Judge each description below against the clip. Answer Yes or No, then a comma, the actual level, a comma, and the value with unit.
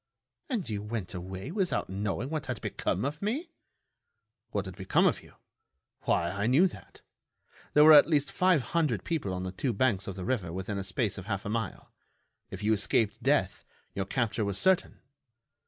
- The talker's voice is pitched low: Yes, low, 110 Hz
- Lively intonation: Yes, wide, 7.2 semitones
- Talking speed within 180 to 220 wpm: Yes, average, 190 wpm